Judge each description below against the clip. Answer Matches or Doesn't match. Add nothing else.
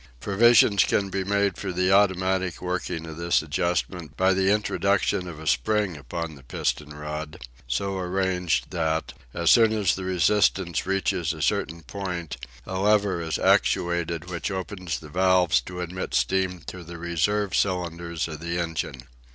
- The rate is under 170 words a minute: Matches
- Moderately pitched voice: Doesn't match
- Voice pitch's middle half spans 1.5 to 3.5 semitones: Matches